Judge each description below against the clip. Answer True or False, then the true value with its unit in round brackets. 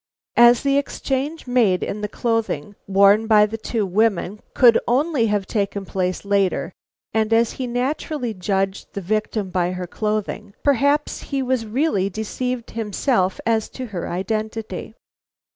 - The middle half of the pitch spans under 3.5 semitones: False (3.8 semitones)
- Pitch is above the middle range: True (215 Hz)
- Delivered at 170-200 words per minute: False (145 wpm)